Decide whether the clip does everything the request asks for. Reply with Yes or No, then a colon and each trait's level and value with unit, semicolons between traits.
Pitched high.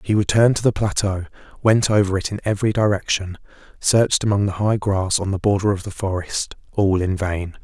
No: low, 100 Hz